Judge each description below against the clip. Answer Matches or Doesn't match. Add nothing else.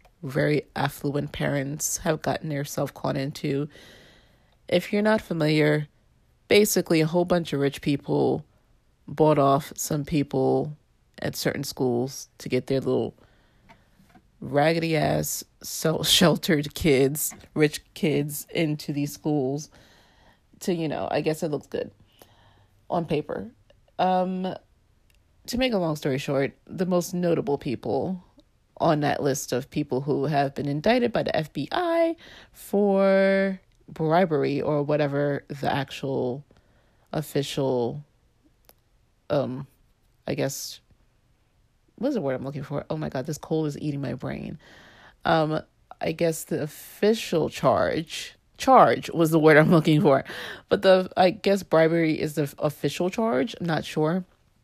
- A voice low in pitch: Doesn't match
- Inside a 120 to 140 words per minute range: Matches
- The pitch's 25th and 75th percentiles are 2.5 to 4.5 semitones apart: Matches